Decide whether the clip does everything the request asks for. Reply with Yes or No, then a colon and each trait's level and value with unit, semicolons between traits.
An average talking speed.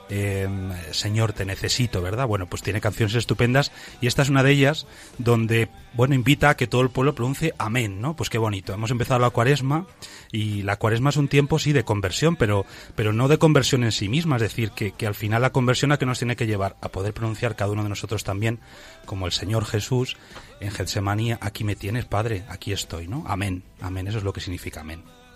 No: fast, 220 wpm